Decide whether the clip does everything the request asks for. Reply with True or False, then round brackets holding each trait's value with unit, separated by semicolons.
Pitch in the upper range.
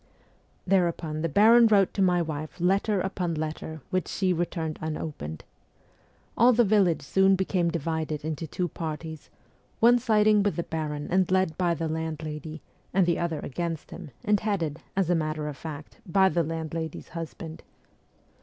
False (170 Hz)